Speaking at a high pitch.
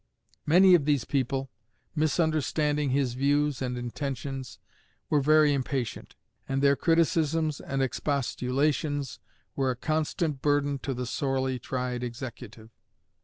No: medium, 140 Hz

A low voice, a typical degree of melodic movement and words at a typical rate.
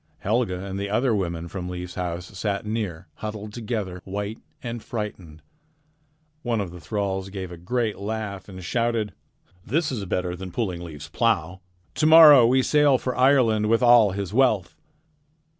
Yes: low, 105 Hz; average, 4.3 semitones; average, 165 wpm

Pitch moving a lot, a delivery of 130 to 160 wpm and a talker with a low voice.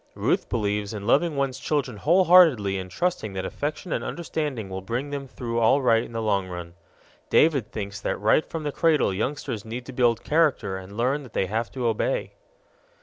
No: wide, 5.9 semitones; average, 200 wpm; low, 120 Hz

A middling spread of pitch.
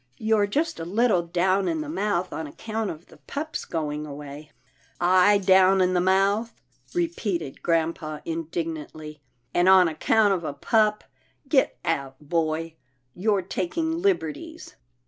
Yes: average, 4.9 semitones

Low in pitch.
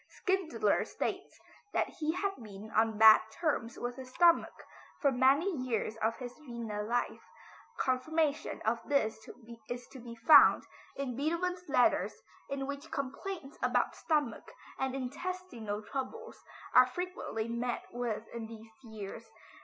No: very high, 255 Hz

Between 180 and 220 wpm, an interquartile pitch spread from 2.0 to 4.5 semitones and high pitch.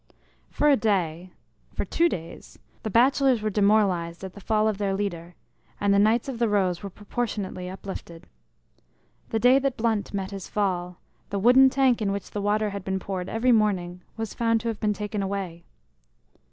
Yes: average, 185 wpm; average, 3.0 semitones; high, 205 Hz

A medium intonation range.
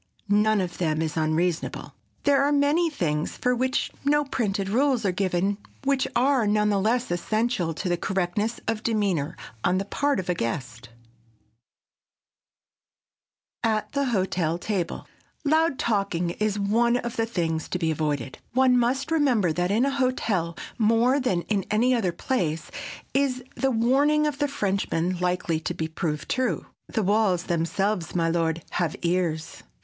No: wide, 6.4 semitones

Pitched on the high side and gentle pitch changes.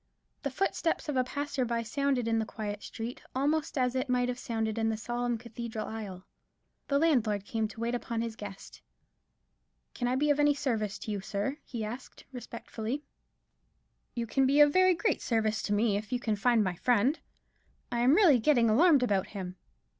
No: high, 240 Hz; average, 3.8 semitones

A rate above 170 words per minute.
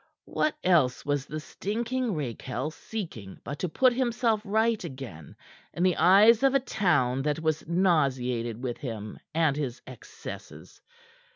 No: average, 145 wpm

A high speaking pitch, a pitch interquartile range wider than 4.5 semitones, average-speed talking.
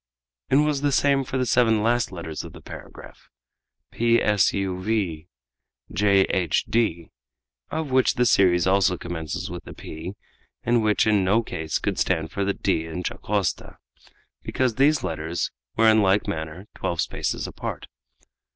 No: low, 100 Hz; average, 5.1 semitones; average, 160 wpm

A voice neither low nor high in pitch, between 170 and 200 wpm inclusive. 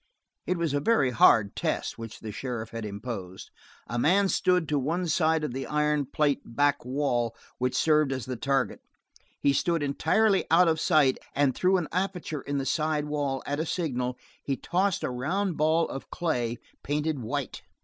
Yes: medium, 145 Hz; average, 180 wpm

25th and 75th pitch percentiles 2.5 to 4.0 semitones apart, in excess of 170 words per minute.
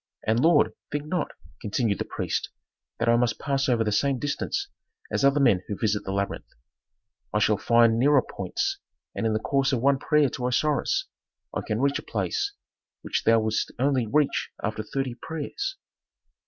No: average, 4.4 semitones; average, 180 wpm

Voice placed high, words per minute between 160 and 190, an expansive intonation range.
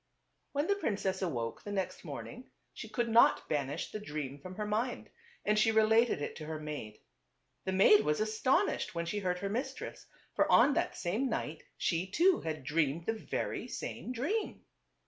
Yes: high, 200 Hz; average, 180 wpm; wide, 6.5 semitones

